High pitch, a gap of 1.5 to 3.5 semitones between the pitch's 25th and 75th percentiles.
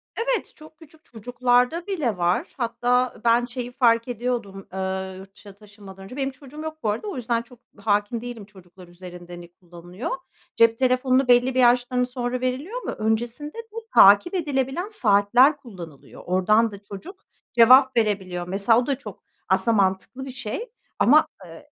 No: high, 240 Hz; average, 4.7 semitones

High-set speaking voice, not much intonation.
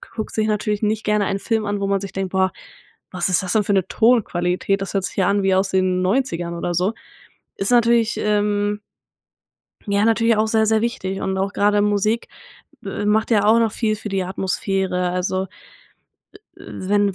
Yes: high, 205 Hz; narrow, 2.3 semitones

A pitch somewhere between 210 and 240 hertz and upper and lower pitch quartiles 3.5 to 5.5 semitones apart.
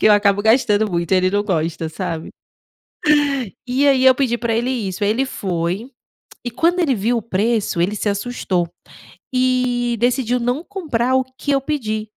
Yes: high, 230 Hz; average, 4.2 semitones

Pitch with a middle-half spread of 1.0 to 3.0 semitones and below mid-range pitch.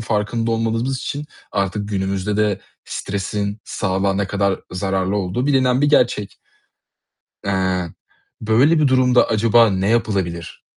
No: average, 3.5 semitones; low, 105 Hz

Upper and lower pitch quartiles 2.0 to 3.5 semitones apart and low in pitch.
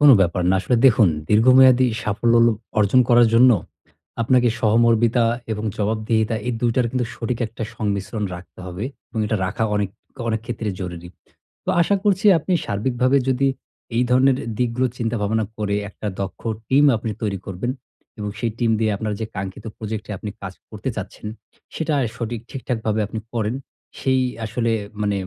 Yes: average, 2.9 semitones; low, 115 Hz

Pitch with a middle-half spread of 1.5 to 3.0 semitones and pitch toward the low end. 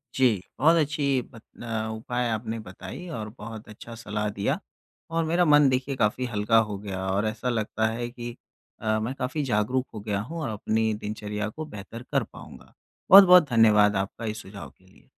No: average, 3.5 semitones; low, 110 Hz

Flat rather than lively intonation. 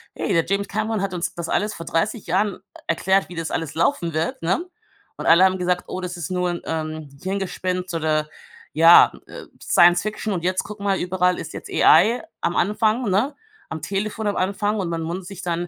No: average, 3.1 semitones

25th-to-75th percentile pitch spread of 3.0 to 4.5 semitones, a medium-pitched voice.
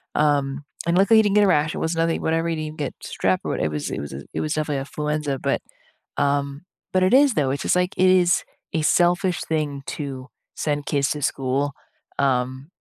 Yes: average, 3.7 semitones; medium, 150 Hz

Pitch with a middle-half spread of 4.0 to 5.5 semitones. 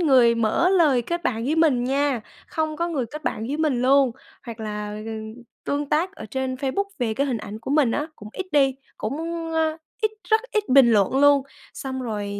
Yes: average, 4.8 semitones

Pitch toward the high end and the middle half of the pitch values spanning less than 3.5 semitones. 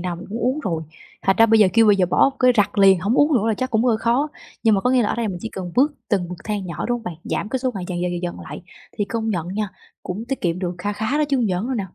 No: high, 210 Hz; average, 4.6 semitones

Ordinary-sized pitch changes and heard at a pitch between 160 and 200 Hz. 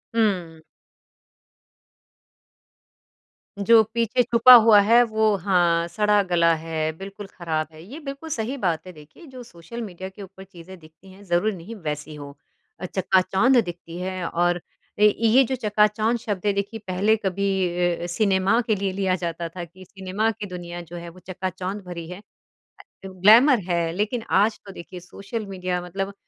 Yes: average, 3.7 semitones; high, 190 Hz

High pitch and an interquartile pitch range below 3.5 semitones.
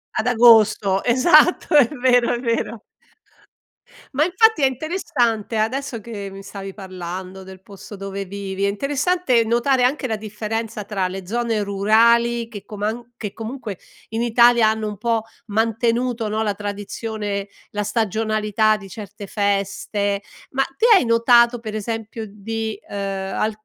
Yes: high, 220 Hz; average, 2.8 semitones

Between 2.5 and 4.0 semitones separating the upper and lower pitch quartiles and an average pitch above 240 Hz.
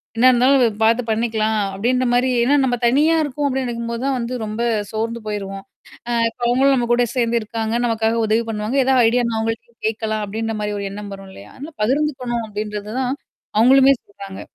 No: average, 2.8 semitones; high, 235 Hz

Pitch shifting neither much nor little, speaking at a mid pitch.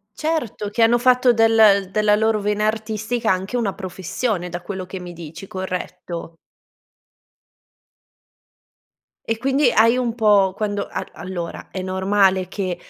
No: average, 3.2 semitones; high, 205 Hz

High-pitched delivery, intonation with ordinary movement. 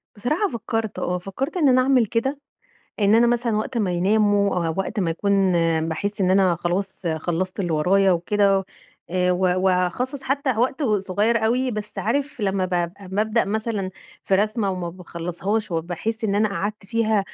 Yes: high, 205 Hz; average, 3.7 semitones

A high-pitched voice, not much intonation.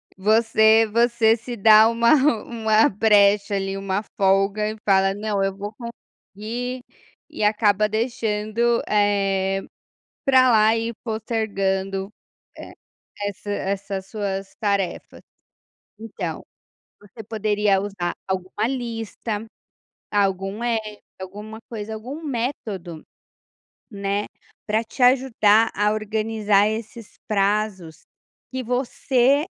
Yes: high, 215 Hz; narrow, 2.3 semitones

